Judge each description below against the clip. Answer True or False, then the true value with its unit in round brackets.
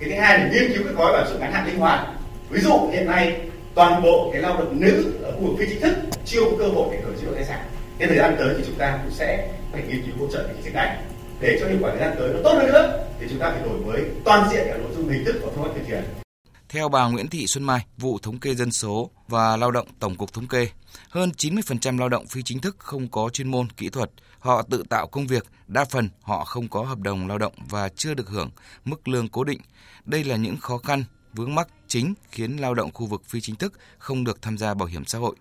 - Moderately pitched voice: False (125 Hz)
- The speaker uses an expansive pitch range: False (4.6 semitones)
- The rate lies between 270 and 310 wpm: True (280 wpm)